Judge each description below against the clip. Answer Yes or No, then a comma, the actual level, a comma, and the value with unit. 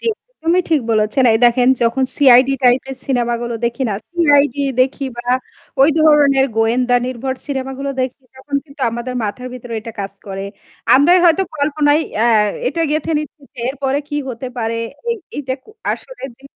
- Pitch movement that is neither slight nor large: Yes, average, 3.3 semitones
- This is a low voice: No, very high, 265 Hz